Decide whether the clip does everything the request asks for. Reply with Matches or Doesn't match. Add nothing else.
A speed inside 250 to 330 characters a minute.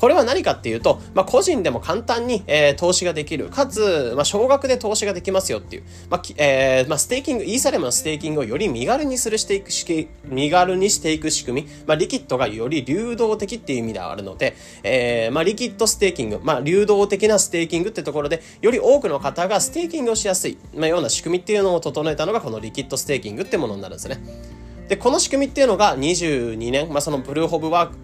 Doesn't match